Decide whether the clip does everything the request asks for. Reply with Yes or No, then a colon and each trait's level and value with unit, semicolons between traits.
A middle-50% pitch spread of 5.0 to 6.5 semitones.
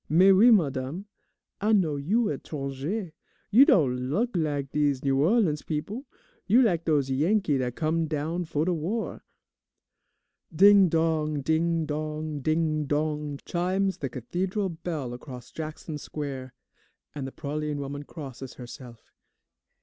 No: average, 4.0 semitones